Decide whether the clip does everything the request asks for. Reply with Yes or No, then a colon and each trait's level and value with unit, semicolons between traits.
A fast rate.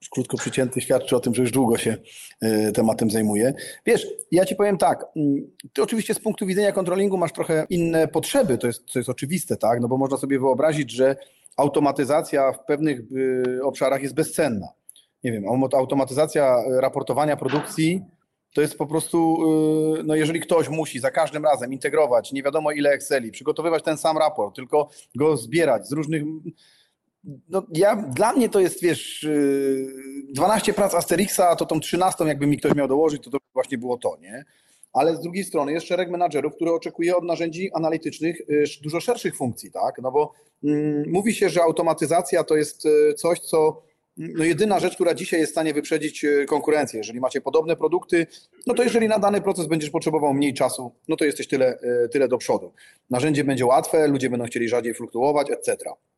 Yes: fast, 175 wpm